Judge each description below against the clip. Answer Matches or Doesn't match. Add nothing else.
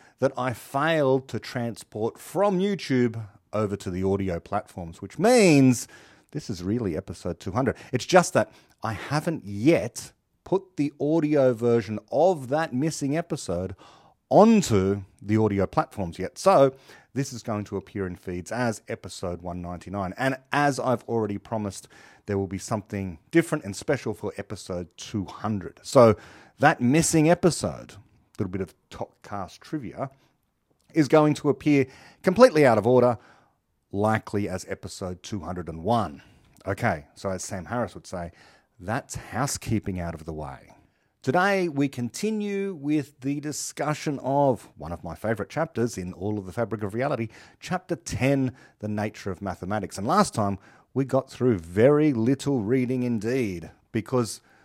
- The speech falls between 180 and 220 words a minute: Doesn't match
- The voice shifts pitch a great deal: Matches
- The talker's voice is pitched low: Matches